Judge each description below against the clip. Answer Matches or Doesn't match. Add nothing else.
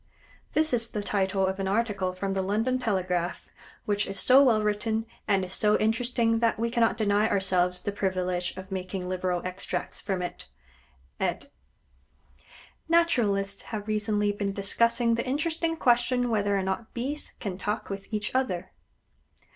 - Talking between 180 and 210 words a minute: Doesn't match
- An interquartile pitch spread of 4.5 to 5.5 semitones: Doesn't match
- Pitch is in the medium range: Doesn't match